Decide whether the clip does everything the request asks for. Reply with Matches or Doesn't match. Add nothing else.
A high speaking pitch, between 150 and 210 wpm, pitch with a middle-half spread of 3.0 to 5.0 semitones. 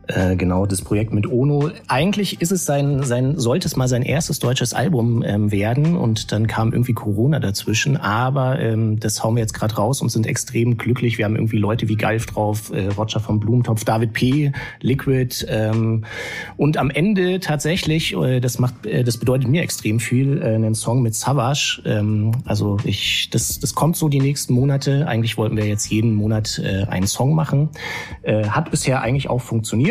Doesn't match